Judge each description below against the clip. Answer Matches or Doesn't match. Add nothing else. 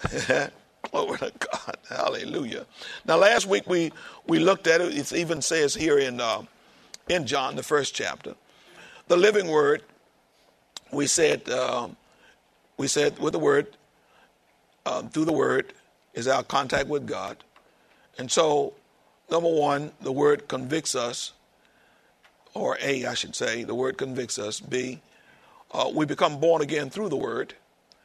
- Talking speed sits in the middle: Matches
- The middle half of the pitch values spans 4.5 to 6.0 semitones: Matches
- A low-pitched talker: Doesn't match